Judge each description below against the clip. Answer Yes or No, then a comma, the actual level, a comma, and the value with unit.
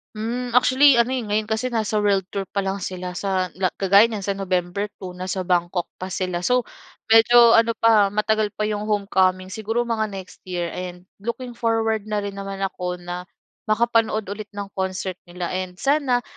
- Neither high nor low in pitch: No, high, 205 Hz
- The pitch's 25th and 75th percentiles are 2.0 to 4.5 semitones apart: Yes, average, 3.4 semitones